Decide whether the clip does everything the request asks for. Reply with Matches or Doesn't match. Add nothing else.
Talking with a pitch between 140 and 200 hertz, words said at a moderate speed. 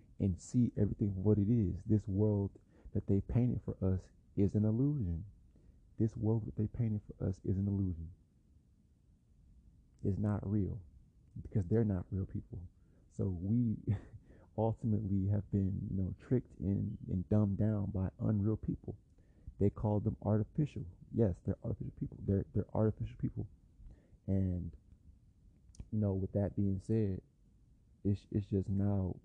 Doesn't match